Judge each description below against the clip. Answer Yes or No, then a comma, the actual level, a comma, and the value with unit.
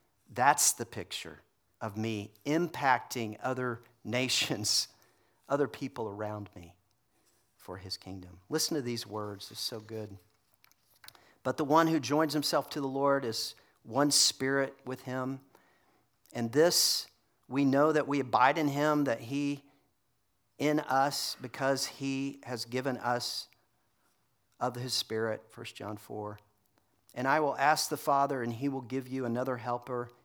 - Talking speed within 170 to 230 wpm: No, average, 145 wpm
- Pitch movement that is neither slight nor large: Yes, average, 3.8 semitones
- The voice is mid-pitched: No, low, 125 Hz